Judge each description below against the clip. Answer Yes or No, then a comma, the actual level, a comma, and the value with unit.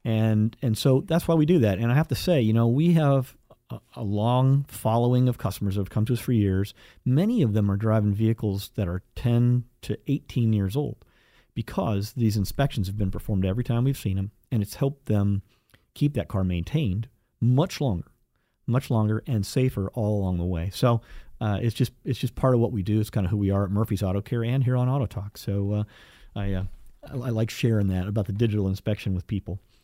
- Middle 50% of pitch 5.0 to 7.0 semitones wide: No, average, 3.8 semitones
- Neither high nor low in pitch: No, low, 110 Hz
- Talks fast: Yes, fast, 225 wpm